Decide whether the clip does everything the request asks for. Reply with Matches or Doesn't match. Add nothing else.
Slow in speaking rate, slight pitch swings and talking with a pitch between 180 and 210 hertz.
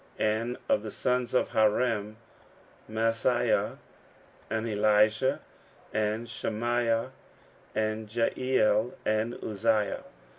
Doesn't match